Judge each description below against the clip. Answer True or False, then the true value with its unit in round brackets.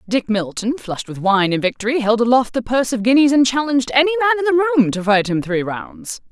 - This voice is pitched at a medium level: False (245 Hz)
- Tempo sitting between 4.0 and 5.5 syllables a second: False (6.4 syllables/s)